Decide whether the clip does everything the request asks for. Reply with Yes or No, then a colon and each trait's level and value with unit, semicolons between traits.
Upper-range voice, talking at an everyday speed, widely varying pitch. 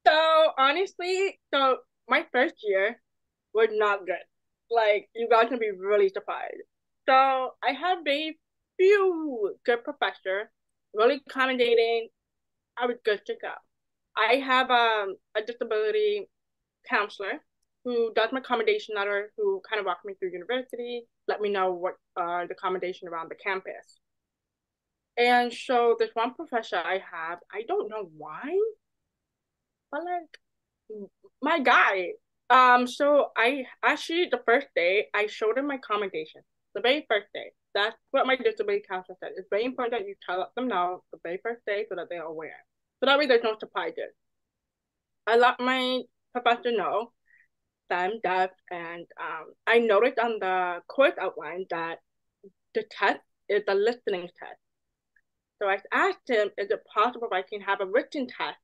Yes: high, 235 Hz; average, 160 wpm; wide, 5.9 semitones